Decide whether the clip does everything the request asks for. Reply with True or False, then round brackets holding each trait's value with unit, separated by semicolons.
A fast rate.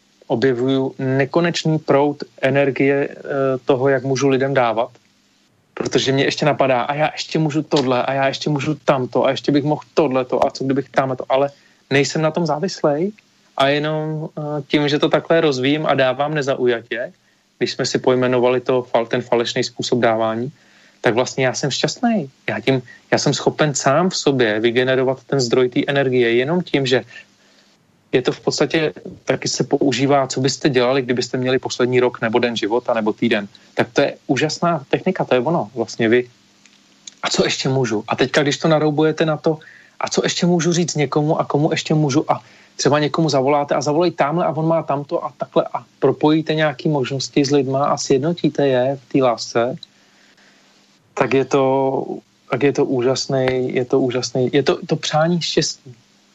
True (180 wpm)